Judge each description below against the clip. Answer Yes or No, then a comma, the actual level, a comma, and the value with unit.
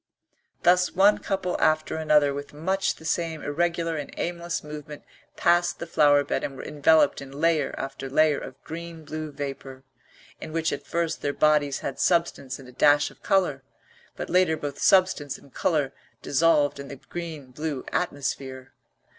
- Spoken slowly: No, average, 165 wpm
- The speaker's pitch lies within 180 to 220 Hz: No, medium, 150 Hz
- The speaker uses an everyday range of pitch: Yes, average, 3.1 semitones